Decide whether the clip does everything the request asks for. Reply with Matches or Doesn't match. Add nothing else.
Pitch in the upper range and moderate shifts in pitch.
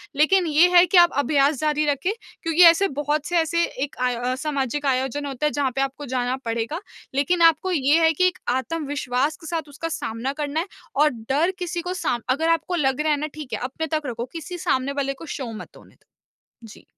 Matches